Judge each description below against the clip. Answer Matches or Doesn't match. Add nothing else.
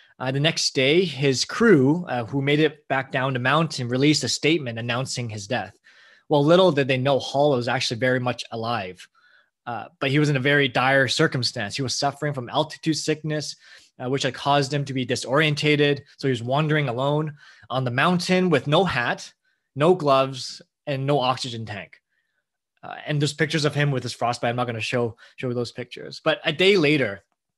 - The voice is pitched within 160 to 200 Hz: Doesn't match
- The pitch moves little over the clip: Doesn't match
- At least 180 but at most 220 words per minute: Matches